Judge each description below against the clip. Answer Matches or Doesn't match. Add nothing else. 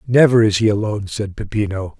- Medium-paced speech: Matches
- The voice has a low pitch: Matches